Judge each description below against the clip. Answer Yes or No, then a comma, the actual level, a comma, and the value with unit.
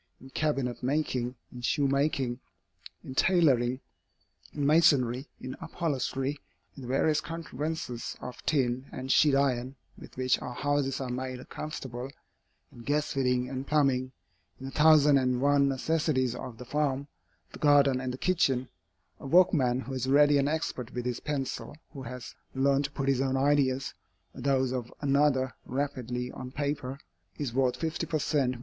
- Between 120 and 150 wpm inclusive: No, average, 160 wpm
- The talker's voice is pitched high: No, low, 135 Hz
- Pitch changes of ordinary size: No, narrow, 2.3 semitones